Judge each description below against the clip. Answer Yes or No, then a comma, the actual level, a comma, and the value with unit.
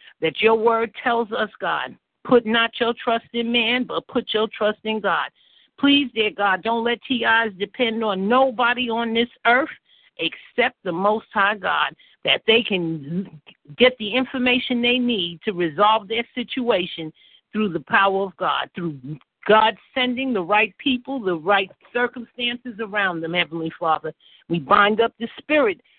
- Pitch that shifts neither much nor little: Yes, average, 3.8 semitones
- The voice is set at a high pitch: Yes, high, 225 Hz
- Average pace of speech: Yes, average, 160 wpm